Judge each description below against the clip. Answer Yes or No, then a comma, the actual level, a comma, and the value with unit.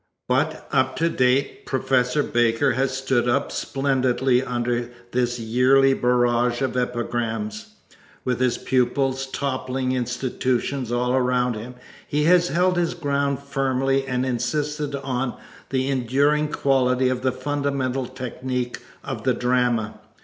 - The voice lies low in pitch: Yes, low, 130 Hz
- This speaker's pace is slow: Yes, slow, 130 wpm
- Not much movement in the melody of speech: Yes, narrow, 1.8 semitones